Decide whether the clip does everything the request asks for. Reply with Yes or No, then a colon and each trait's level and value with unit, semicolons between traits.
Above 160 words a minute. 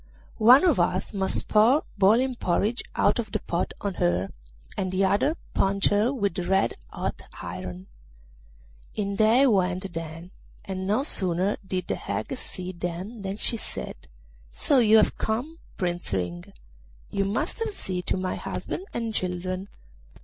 No: average, 155 wpm